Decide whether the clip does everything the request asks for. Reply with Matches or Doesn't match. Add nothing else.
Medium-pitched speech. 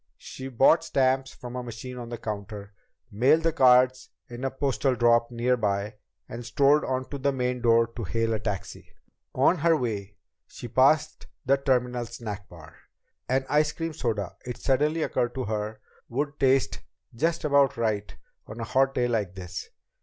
Doesn't match